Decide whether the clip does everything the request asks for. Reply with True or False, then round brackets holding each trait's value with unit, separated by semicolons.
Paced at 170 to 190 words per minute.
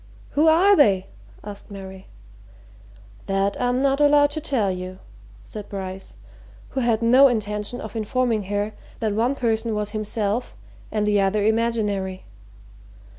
False (135 wpm)